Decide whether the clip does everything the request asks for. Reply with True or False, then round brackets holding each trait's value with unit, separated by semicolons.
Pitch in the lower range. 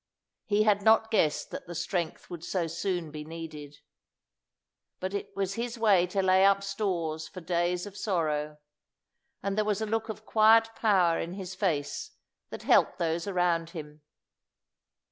False (185 Hz)